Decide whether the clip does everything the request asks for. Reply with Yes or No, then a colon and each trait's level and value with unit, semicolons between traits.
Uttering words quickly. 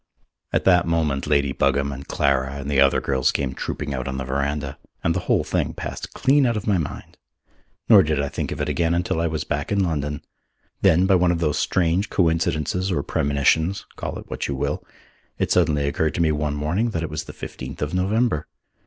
Yes: fast, 215 wpm